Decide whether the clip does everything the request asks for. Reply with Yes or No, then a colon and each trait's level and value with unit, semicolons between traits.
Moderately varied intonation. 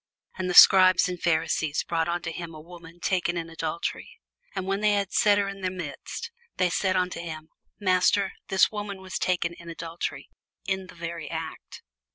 No: narrow, 2.2 semitones